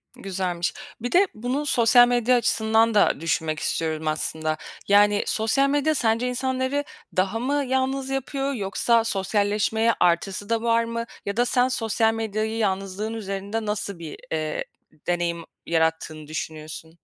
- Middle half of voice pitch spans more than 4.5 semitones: Yes, average, 5.1 semitones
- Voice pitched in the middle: No, high, 220 Hz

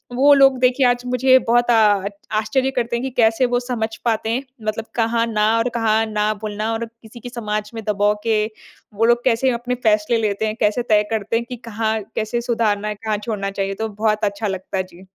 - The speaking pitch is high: Yes, high, 225 Hz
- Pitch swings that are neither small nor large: No, narrow, 2.2 semitones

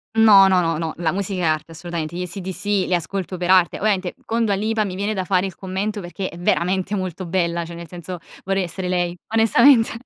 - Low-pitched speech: No, medium, 185 Hz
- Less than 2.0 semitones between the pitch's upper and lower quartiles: No, narrow, 2.4 semitones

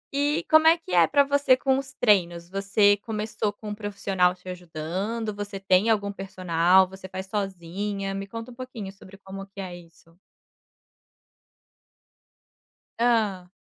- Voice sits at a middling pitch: No, high, 195 Hz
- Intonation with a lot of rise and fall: No, average, 3.3 semitones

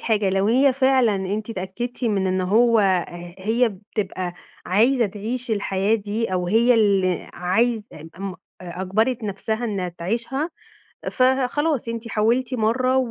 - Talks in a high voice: Yes, high, 220 Hz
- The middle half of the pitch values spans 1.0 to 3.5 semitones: No, average, 4.1 semitones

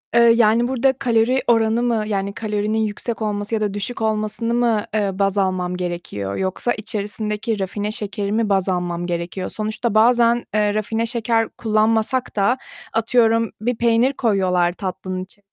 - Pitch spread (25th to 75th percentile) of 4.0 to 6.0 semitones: No, average, 2.7 semitones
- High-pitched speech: Yes, high, 215 Hz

